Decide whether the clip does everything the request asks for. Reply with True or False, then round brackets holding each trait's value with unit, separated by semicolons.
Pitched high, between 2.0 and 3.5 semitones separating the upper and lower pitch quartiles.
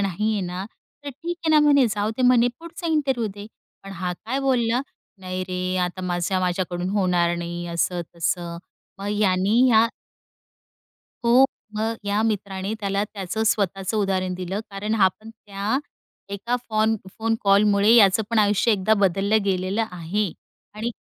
True (200 Hz; 3.2 semitones)